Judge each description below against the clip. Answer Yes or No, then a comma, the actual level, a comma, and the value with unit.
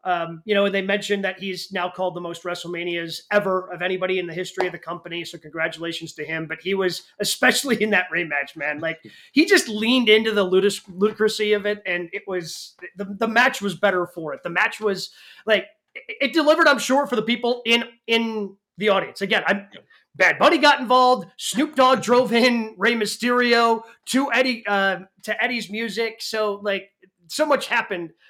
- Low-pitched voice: No, high, 205 Hz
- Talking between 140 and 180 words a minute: No, average, 200 wpm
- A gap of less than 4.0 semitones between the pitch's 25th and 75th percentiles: No, average, 4.3 semitones